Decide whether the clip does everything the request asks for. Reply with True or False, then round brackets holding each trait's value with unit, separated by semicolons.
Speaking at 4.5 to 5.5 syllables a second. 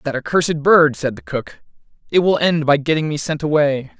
True (5.4 syllables/s)